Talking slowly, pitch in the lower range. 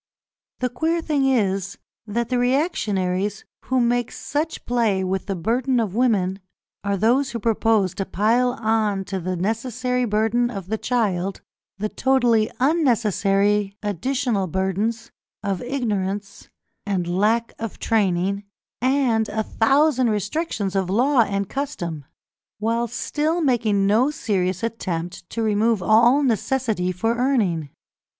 No: slow, 130 wpm; high, 220 Hz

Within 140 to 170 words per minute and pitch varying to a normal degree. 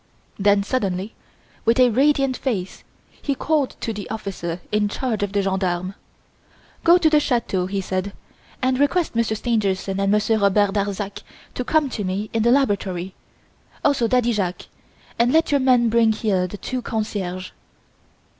Yes: average, 160 wpm; average, 4.4 semitones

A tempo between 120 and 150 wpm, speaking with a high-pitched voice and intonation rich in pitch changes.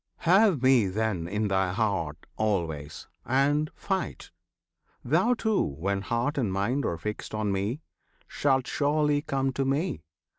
No: average, 140 wpm; low, 120 Hz; wide, 6.9 semitones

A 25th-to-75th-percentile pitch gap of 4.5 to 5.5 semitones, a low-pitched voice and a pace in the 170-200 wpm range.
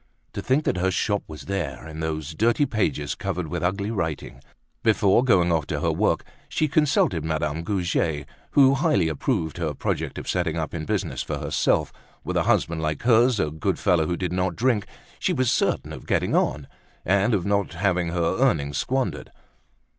Yes: average, 4.9 semitones; very low, 90 Hz; average, 185 wpm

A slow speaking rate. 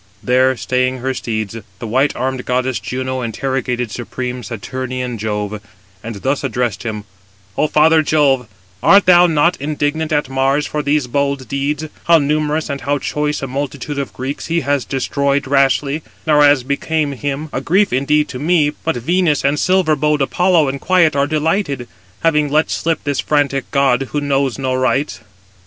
No: average, 165 wpm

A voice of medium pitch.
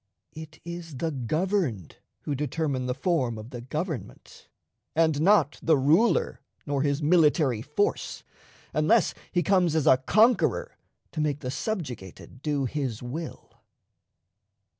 Yes: medium, 150 Hz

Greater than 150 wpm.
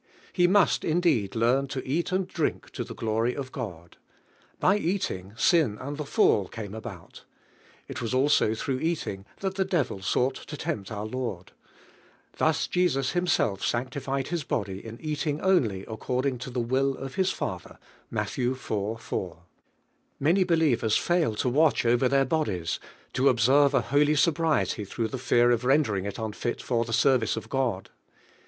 Yes: average, 175 wpm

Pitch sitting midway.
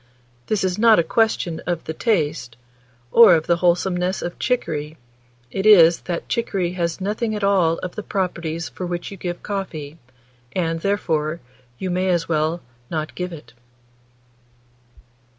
Yes: medium, 175 Hz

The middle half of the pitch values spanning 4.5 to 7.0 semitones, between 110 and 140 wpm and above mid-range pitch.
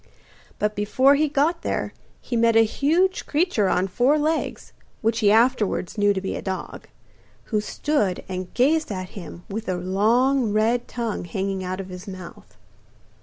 No: wide, 5.6 semitones; average, 170 wpm; high, 215 Hz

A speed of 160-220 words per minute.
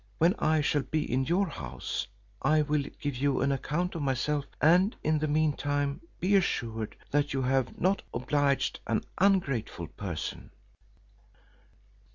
No: average, 150 wpm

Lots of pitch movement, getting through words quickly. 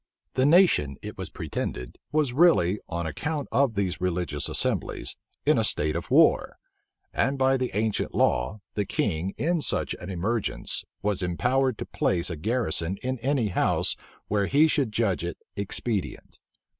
No: wide, 7.0 semitones; average, 155 wpm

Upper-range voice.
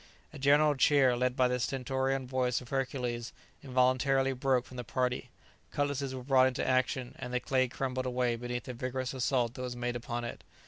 No: low, 130 Hz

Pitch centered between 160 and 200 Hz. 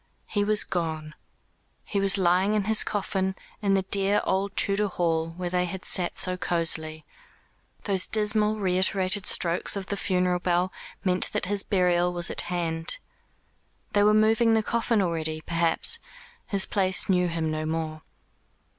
Yes: medium, 185 Hz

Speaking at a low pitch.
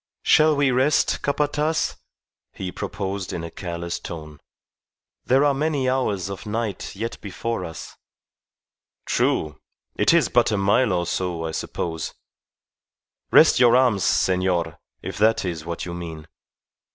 Yes: low, 100 Hz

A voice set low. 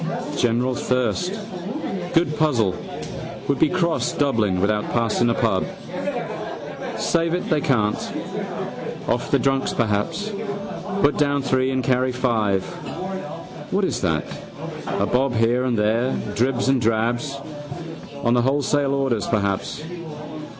Yes: low, 125 Hz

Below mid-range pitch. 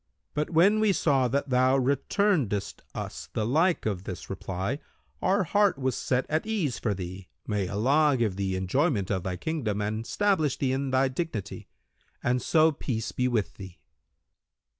Yes: low, 130 Hz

